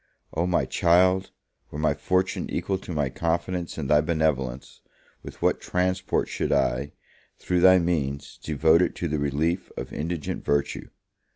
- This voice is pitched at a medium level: No, very low, 80 Hz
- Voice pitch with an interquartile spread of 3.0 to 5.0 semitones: Yes, average, 3.6 semitones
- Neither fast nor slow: Yes, average, 155 wpm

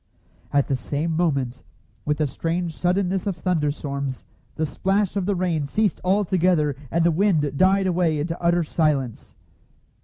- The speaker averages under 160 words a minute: Yes, average, 150 wpm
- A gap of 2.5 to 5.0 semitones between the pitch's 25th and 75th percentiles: Yes, average, 3.9 semitones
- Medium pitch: Yes, medium, 165 Hz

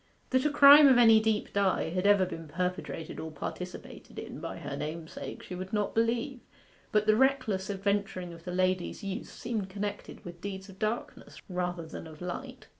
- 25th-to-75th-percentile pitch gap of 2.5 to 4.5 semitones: Yes, average, 3.6 semitones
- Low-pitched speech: No, high, 195 Hz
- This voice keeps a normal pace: Yes, average, 185 wpm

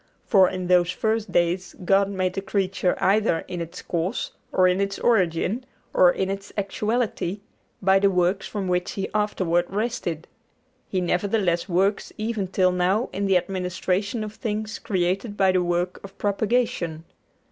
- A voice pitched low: No, high, 190 Hz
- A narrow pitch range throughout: Yes, narrow, 2.3 semitones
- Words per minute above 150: Yes, average, 160 wpm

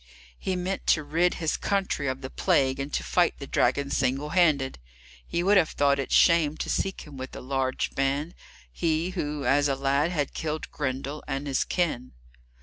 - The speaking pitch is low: No, medium, 145 Hz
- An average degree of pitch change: Yes, average, 3.6 semitones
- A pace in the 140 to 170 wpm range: No, average, 190 wpm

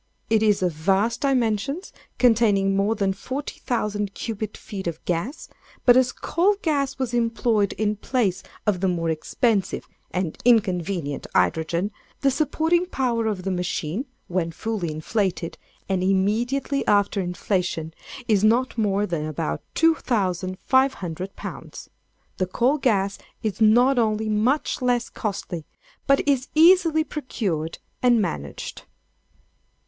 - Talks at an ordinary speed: No, slow, 125 wpm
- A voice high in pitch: Yes, high, 210 Hz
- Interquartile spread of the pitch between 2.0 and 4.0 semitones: No, average, 5.2 semitones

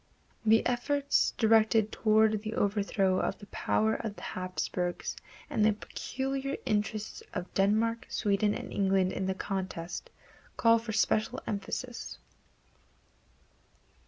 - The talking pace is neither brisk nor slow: No, slow, 120 wpm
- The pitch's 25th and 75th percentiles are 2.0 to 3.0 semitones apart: Yes, narrow, 2.5 semitones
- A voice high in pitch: Yes, high, 215 Hz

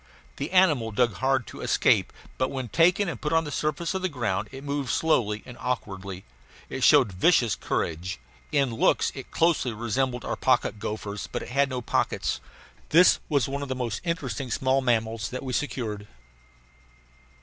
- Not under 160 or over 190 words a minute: Yes, average, 175 wpm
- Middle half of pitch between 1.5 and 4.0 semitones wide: No, average, 4.5 semitones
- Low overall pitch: Yes, low, 130 Hz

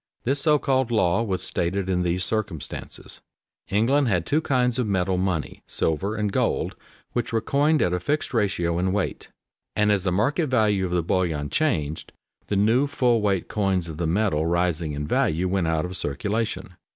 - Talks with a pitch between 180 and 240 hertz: No, very low, 95 Hz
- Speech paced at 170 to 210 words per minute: Yes, average, 190 wpm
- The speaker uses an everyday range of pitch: Yes, average, 4.8 semitones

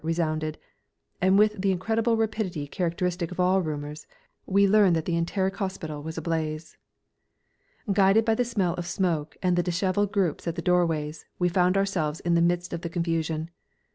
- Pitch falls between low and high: Yes, medium, 175 Hz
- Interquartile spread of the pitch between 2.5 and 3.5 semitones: Yes, average, 3.0 semitones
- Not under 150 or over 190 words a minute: Yes, average, 170 wpm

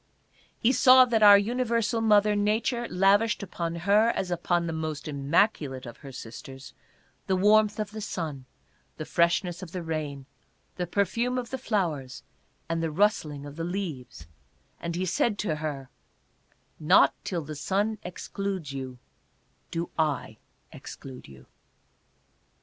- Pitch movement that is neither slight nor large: No, wide, 5.8 semitones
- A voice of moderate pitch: Yes, medium, 175 Hz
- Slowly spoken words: No, average, 150 wpm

